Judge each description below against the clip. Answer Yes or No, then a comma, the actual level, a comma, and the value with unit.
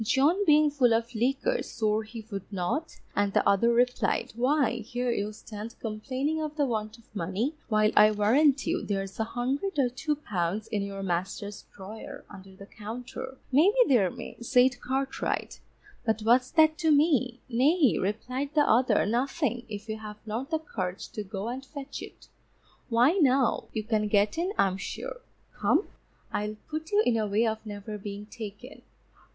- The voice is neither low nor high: No, high, 235 Hz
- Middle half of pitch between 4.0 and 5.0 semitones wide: Yes, average, 4.7 semitones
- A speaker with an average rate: Yes, average, 175 wpm